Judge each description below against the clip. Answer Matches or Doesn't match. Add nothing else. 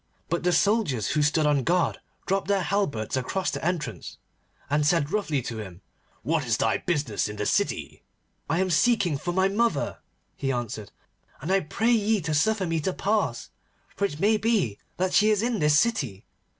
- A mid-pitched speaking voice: Matches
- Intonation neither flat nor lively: Doesn't match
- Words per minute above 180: Matches